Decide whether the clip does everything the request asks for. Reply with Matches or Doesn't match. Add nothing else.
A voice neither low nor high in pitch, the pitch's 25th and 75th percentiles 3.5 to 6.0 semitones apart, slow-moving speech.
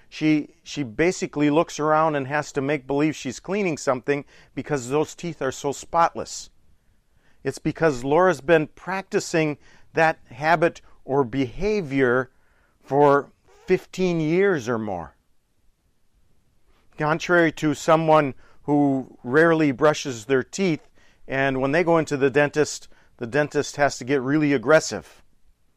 Doesn't match